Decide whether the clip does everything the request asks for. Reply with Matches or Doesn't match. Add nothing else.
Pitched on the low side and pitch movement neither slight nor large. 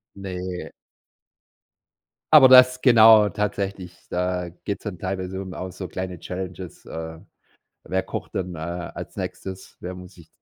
Doesn't match